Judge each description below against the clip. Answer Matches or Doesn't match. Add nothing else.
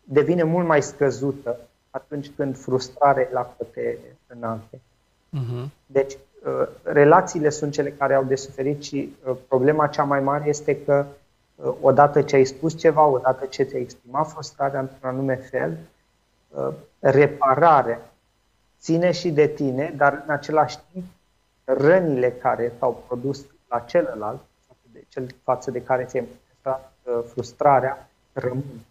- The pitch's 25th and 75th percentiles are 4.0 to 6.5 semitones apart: Doesn't match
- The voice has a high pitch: Doesn't match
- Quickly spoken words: Doesn't match